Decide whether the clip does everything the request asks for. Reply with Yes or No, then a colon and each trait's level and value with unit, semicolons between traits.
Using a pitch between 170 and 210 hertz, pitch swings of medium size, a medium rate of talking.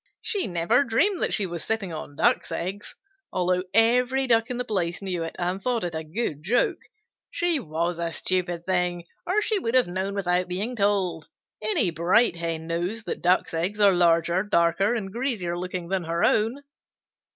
Yes: medium, 185 Hz; average, 4.8 semitones; average, 185 wpm